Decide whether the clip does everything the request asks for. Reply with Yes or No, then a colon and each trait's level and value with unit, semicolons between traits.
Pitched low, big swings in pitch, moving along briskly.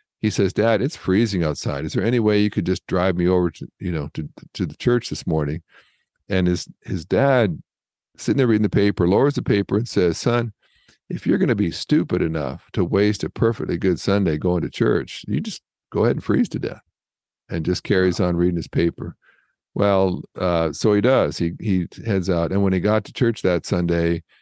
No: very low, 95 Hz; average, 3.1 semitones; fast, 215 wpm